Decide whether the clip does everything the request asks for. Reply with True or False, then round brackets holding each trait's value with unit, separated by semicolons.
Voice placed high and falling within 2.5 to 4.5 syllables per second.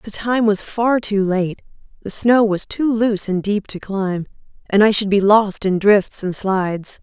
True (205 Hz; 4.3 syllables/s)